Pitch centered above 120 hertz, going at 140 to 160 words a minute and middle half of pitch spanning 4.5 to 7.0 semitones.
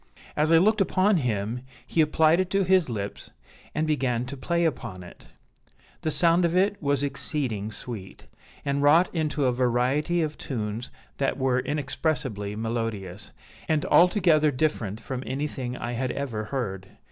Yes: medium, 140 Hz; average, 155 wpm; average, 5.3 semitones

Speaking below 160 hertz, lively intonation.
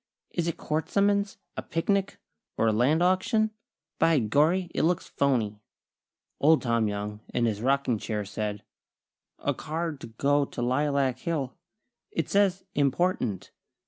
Yes: medium, 140 Hz; wide, 6.7 semitones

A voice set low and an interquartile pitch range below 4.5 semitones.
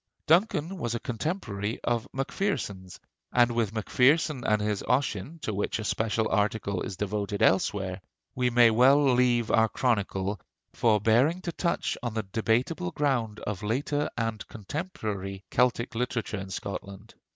Yes: low, 115 Hz; average, 3.7 semitones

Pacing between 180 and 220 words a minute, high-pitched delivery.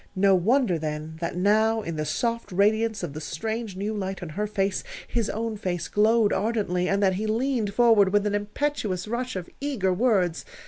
Yes: average, 190 wpm; high, 205 Hz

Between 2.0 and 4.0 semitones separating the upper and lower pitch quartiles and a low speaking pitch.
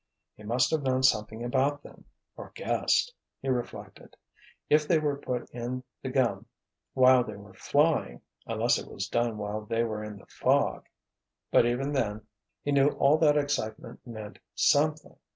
No: average, 4.7 semitones; low, 125 Hz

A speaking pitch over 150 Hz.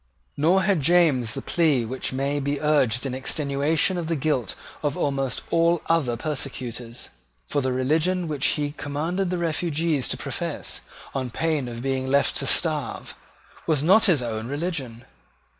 No: medium, 145 Hz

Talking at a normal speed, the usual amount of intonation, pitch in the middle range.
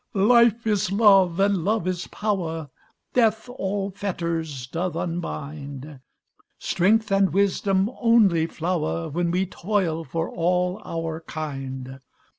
No: slow, 115 wpm; average, 3.9 semitones; medium, 180 Hz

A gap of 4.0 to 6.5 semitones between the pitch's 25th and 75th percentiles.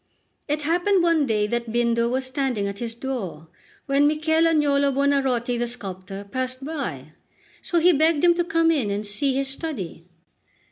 Yes: average, 5.0 semitones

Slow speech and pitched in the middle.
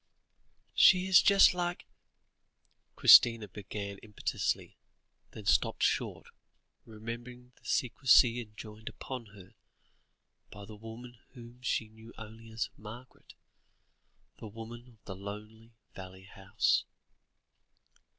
No: slow, 110 wpm; low, 110 Hz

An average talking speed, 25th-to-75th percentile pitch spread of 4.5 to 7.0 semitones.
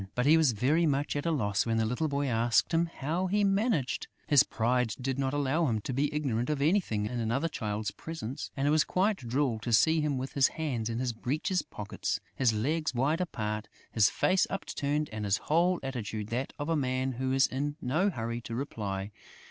No: fast, 210 wpm; average, 5.1 semitones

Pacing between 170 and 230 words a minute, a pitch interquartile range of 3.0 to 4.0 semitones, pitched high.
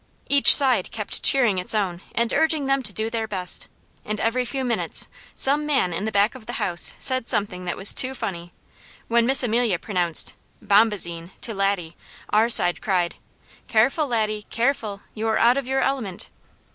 No: average, 175 wpm; average, 4.7 semitones; high, 220 Hz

